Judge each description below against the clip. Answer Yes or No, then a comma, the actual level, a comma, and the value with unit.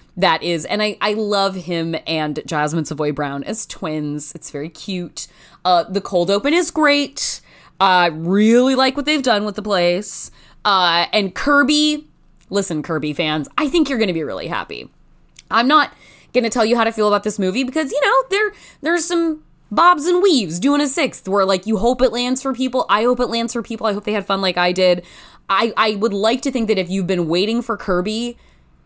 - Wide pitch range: Yes, wide, 6.7 semitones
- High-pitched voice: Yes, high, 210 Hz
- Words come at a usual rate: No, fast, 220 wpm